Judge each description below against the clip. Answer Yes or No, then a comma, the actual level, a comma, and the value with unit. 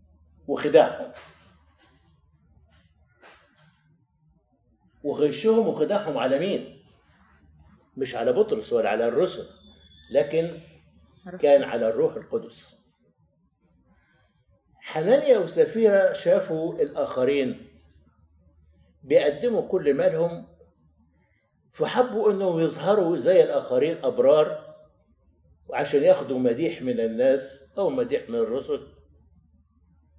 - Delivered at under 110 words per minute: Yes, average, 75 wpm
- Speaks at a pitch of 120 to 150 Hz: Yes, medium, 140 Hz